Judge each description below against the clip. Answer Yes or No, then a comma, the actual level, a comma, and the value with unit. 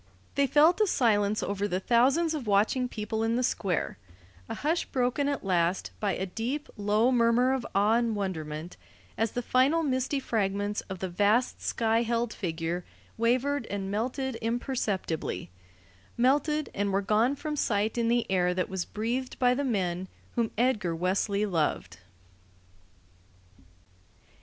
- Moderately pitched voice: No, high, 225 Hz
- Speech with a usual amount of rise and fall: Yes, average, 4.6 semitones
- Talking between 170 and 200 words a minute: No, average, 150 wpm